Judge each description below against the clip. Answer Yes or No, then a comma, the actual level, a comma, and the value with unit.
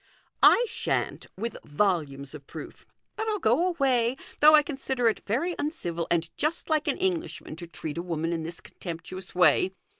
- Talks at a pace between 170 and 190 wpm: Yes, average, 180 wpm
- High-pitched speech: Yes, high, 205 Hz